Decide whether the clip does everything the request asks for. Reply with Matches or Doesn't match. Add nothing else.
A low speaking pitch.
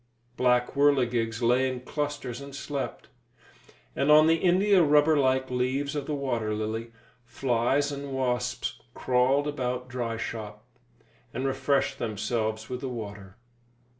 Matches